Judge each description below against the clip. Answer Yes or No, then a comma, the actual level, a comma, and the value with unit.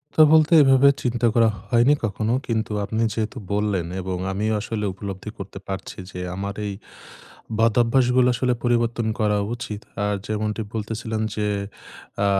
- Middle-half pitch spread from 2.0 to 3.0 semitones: Yes, narrow, 2.6 semitones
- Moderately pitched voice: No, low, 110 Hz